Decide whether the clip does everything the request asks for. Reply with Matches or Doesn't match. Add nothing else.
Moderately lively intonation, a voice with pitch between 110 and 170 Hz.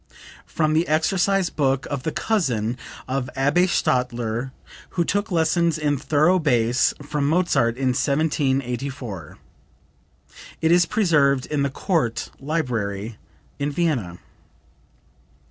Matches